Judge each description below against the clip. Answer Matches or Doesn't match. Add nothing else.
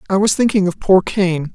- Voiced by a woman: Matches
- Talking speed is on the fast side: Matches